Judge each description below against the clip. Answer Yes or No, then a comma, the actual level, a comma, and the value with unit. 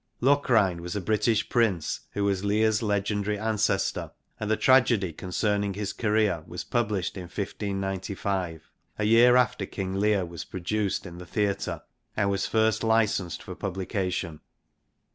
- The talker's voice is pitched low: Yes, low, 100 Hz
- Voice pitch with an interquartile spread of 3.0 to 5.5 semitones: No, narrow, 2.5 semitones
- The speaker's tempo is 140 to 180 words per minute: Yes, average, 145 wpm